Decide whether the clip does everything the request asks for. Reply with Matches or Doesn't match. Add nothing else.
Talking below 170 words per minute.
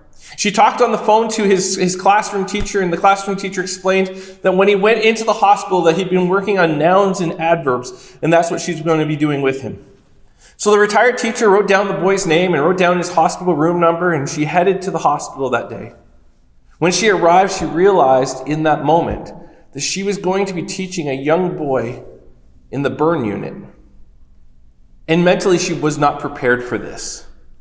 Doesn't match